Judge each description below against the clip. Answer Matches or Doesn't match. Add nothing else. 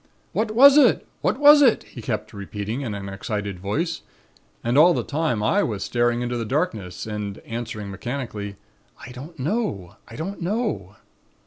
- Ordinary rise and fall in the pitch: Doesn't match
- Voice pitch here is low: Matches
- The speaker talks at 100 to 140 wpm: Doesn't match